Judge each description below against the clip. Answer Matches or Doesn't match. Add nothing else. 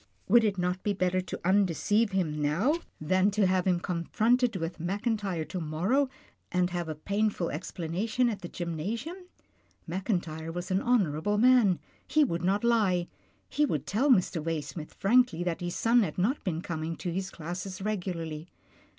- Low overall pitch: Doesn't match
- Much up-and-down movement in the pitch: Doesn't match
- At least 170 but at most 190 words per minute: Matches